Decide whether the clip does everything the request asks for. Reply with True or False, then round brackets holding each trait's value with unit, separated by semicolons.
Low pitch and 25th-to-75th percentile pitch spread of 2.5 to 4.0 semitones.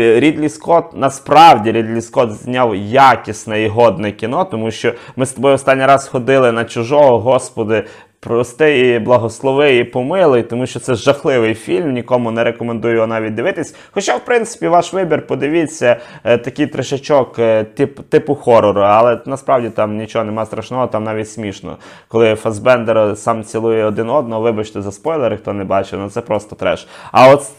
True (120 Hz; 3.4 semitones)